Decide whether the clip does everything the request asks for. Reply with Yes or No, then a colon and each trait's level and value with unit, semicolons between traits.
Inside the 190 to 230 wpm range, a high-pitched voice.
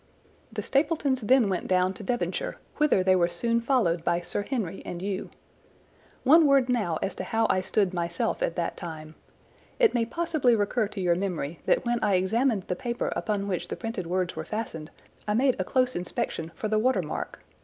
Yes: average, 195 wpm; high, 205 Hz